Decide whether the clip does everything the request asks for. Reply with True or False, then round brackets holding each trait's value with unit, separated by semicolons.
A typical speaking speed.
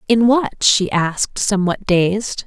True (145 wpm)